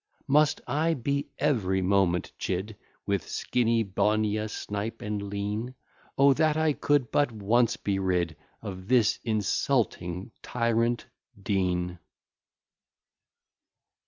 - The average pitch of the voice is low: Yes, low, 110 Hz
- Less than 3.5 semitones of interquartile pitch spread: No, average, 4.2 semitones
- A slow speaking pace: Yes, slow, 100 wpm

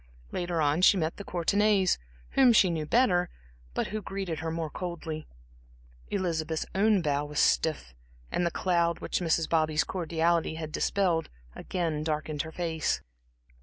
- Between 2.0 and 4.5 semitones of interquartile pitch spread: Yes, average, 2.7 semitones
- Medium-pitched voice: Yes, medium, 170 Hz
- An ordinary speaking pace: Yes, average, 150 wpm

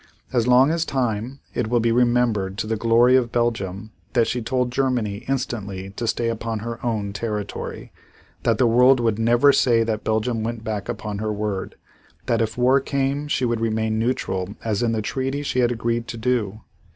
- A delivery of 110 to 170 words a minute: No, average, 190 wpm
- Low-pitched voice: Yes, low, 115 Hz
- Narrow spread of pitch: Yes, narrow, 2.3 semitones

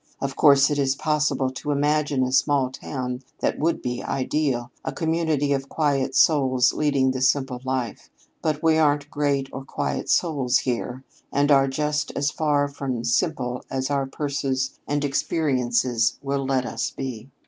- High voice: No, low, 135 Hz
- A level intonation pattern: Yes, narrow, 2.1 semitones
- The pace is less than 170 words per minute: Yes, average, 160 wpm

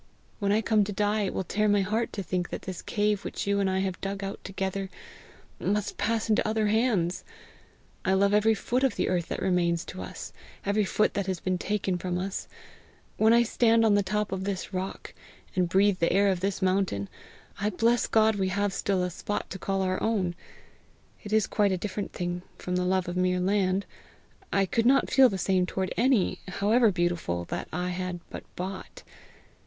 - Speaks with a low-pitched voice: No, high, 195 Hz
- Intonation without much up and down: Yes, narrow, 2.3 semitones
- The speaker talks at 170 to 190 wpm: No, fast, 205 wpm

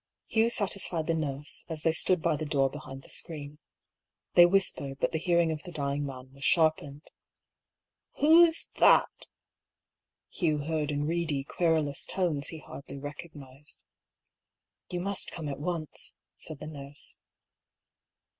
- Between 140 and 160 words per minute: Yes, average, 145 wpm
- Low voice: No, medium, 155 Hz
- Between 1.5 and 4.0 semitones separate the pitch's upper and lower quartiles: Yes, average, 3.1 semitones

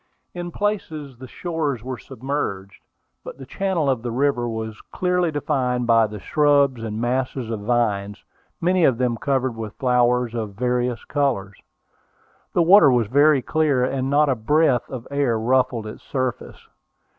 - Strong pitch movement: No, average, 3.8 semitones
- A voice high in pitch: No, low, 130 Hz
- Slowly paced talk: No, average, 155 wpm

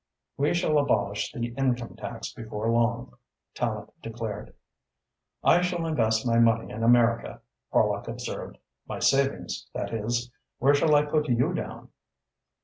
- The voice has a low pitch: Yes, low, 120 Hz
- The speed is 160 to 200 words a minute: No, average, 140 wpm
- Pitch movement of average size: Yes, average, 3.8 semitones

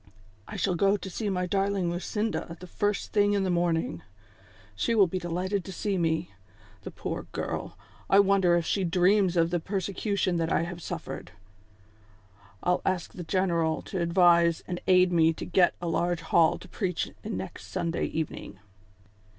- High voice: No, medium, 180 Hz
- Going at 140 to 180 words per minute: Yes, average, 175 wpm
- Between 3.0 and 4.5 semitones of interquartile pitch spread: No, narrow, 2.4 semitones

